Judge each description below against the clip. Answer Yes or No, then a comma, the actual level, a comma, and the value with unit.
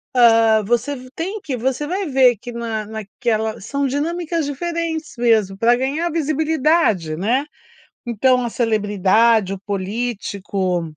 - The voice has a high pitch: Yes, high, 240 Hz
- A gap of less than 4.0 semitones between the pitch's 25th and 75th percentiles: No, average, 5.2 semitones